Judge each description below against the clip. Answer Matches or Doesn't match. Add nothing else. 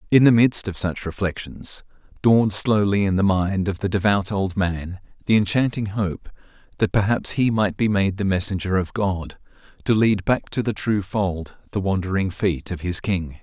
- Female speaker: Doesn't match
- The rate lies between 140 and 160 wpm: Doesn't match